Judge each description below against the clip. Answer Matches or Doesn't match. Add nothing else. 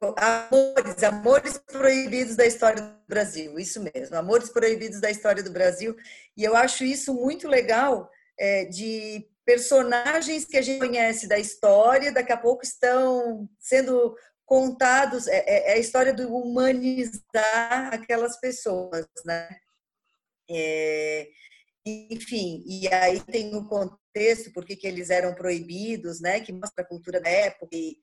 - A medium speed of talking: Matches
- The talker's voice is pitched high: Matches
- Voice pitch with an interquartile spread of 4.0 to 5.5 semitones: Matches